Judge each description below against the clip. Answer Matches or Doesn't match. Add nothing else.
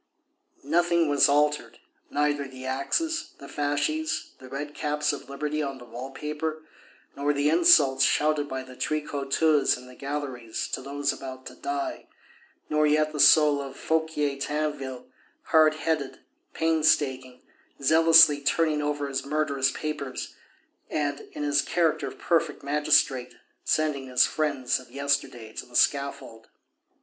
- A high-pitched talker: Doesn't match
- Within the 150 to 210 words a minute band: Doesn't match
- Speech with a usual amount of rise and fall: Doesn't match